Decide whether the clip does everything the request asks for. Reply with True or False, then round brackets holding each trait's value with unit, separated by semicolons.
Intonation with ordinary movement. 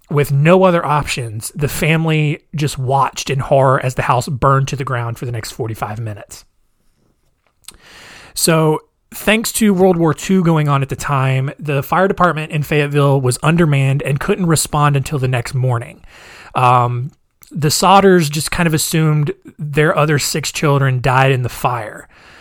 True (3.2 semitones)